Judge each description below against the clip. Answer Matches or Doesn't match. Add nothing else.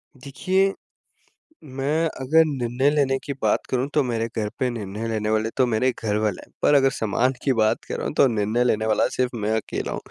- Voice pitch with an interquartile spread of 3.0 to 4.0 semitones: Matches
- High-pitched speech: Doesn't match